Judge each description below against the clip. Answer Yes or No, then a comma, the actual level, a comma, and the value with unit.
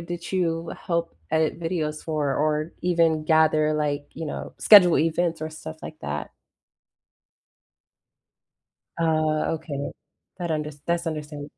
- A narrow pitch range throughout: Yes, narrow, 1.7 semitones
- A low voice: No, medium, 160 Hz